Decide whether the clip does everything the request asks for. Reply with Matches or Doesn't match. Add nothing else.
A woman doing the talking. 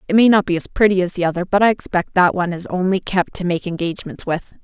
Matches